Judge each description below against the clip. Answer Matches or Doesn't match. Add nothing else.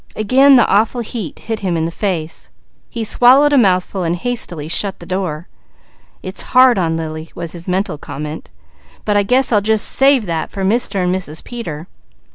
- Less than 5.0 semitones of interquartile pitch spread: Doesn't match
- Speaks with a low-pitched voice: Doesn't match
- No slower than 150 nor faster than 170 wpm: Doesn't match